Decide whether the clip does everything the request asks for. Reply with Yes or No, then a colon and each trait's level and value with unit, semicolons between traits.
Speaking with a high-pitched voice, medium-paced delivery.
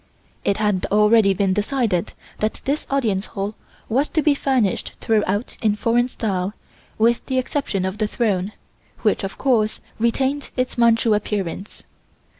Yes: high, 215 Hz; average, 145 wpm